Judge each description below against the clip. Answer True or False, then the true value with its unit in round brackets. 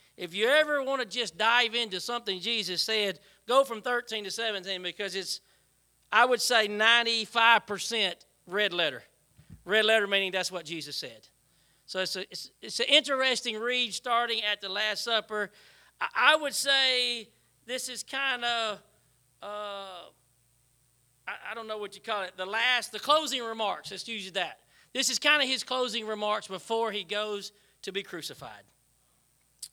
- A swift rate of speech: False (165 wpm)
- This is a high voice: True (215 Hz)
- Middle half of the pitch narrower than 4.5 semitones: True (3.8 semitones)